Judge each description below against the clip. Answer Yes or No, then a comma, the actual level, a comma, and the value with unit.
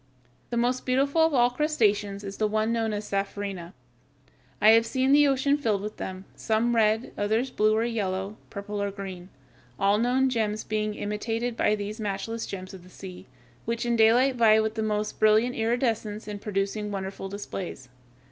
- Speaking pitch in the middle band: No, high, 215 Hz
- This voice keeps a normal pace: Yes, average, 175 wpm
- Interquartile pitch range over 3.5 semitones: No, average, 2.7 semitones